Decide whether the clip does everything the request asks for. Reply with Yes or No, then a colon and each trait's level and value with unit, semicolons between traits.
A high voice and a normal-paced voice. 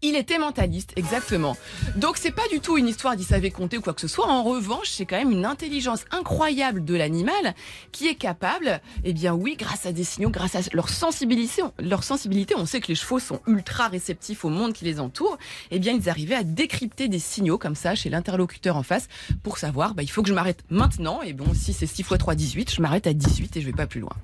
No: high, 195 Hz; fast, 250 wpm